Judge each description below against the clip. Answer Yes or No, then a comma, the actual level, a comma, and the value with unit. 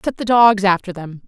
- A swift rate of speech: Yes, fast, 235 wpm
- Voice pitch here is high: Yes, high, 205 Hz